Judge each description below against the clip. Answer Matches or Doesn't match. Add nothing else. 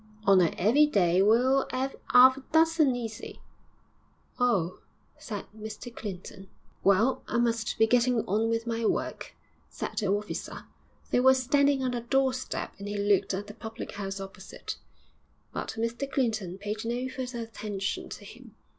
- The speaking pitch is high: Matches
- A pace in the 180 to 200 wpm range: Doesn't match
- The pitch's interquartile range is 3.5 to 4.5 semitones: Matches